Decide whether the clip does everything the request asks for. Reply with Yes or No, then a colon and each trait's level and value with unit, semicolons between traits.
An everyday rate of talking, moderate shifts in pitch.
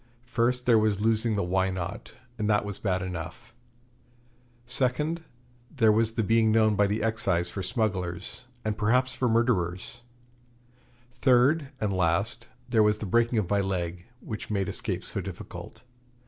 Yes: average, 155 wpm; average, 3.6 semitones